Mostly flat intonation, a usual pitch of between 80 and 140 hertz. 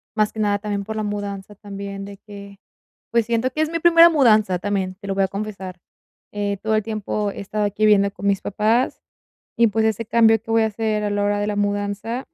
No: narrow, 1.7 semitones; high, 205 Hz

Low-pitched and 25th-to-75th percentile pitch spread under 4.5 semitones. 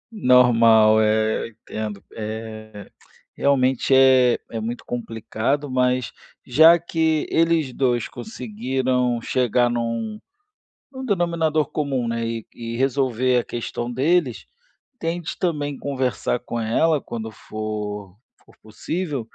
Yes: low, 125 Hz; average, 4.1 semitones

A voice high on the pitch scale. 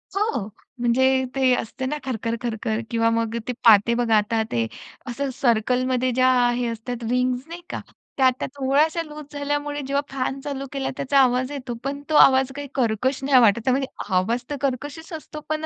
Yes: very high, 255 Hz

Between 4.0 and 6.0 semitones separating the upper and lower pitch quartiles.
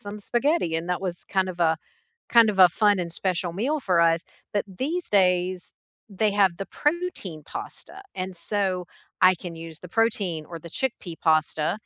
No: average, 3.5 semitones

